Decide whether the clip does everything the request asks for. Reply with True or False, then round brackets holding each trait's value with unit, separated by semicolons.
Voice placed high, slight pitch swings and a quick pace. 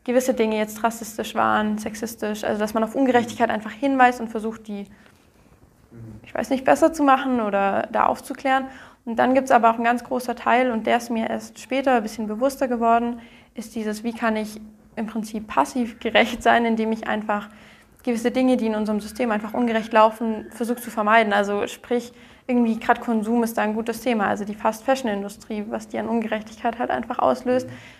True (230 Hz; 2.0 semitones; 195 wpm)